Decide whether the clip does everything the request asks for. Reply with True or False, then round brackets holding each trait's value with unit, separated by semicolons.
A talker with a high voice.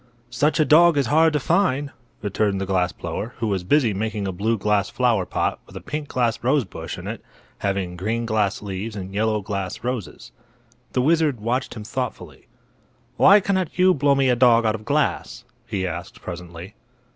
False (110 Hz)